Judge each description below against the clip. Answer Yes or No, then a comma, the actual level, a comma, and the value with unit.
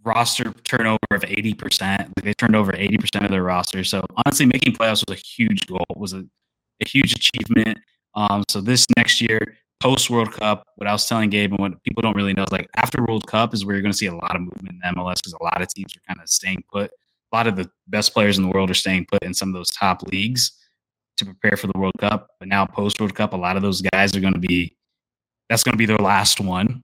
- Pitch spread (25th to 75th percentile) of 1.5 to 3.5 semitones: Yes, average, 2.7 semitones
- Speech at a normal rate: No, fast, 255 wpm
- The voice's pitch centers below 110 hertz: Yes, low, 100 Hz